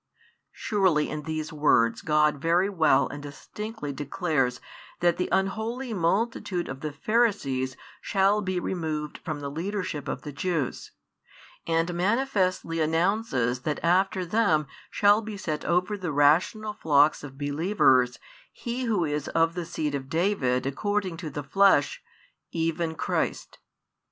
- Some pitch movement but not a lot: Yes, average, 5.0 semitones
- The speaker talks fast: No, average, 140 wpm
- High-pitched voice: No, medium, 165 Hz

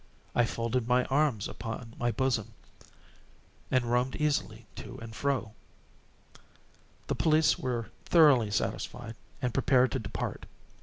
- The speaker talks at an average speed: No, slow, 120 wpm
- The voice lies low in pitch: Yes, low, 120 Hz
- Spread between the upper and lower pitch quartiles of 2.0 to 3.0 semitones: Yes, average, 2.7 semitones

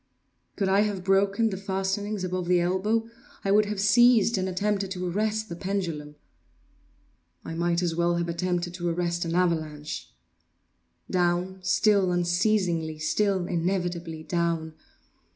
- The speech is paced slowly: Yes, slow, 130 wpm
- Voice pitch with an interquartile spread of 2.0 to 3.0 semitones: Yes, narrow, 2.5 semitones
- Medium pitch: Yes, medium, 180 Hz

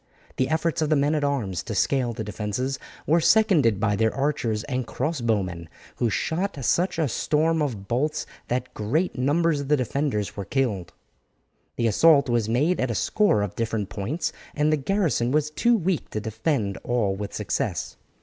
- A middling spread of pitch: No, wide, 6.0 semitones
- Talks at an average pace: Yes, average, 180 wpm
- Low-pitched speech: Yes, low, 130 Hz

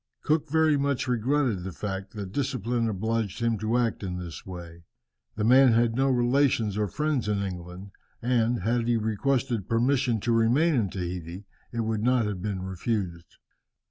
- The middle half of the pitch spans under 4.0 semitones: No, average, 4.3 semitones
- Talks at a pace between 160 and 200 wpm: Yes, average, 170 wpm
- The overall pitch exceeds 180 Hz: No, low, 115 Hz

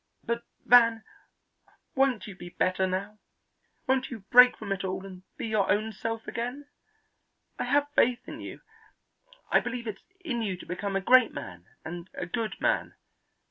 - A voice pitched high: Yes, high, 220 Hz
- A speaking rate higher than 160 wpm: Yes, average, 170 wpm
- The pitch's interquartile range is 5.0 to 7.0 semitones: No, average, 4.4 semitones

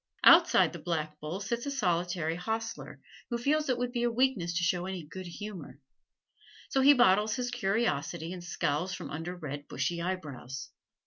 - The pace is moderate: Yes, average, 175 wpm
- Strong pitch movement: Yes, wide, 6.3 semitones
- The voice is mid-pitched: Yes, medium, 180 Hz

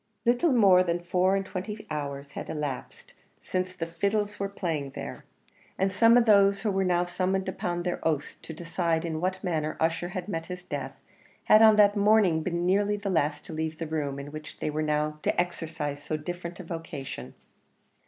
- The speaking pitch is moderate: Yes, medium, 175 Hz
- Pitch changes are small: No, average, 3.8 semitones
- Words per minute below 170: No, average, 195 wpm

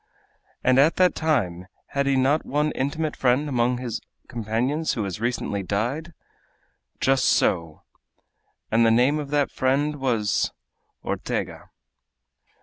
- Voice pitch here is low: Yes, low, 130 Hz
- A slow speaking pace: Yes, slow, 125 wpm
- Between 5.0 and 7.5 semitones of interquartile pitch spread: No, average, 4.3 semitones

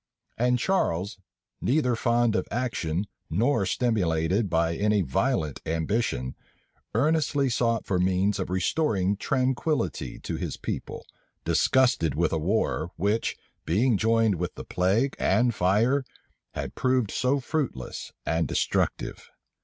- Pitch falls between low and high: No, low, 105 Hz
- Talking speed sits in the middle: No, slow, 120 wpm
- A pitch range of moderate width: No, wide, 5.7 semitones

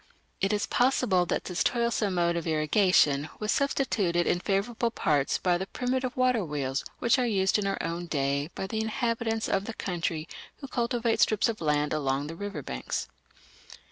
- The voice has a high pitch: Yes, high, 195 Hz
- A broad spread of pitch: Yes, wide, 5.9 semitones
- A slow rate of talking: No, average, 175 wpm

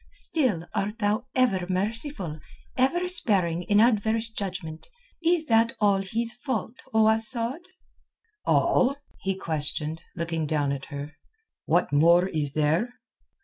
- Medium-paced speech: No, slow, 125 wpm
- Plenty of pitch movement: Yes, wide, 6.1 semitones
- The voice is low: No, high, 205 Hz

